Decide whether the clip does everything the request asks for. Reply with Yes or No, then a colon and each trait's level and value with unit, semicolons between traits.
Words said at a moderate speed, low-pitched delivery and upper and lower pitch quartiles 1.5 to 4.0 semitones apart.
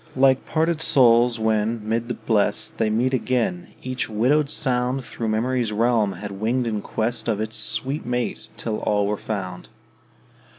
Yes: average, 160 wpm; low, 115 Hz; average, 2.9 semitones